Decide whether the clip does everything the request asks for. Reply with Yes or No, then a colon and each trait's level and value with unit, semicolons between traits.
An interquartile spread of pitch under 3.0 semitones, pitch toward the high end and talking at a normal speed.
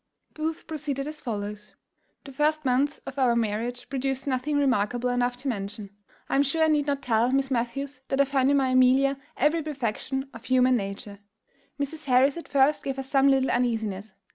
Yes: narrow, 2.6 semitones; very high, 265 Hz; average, 190 wpm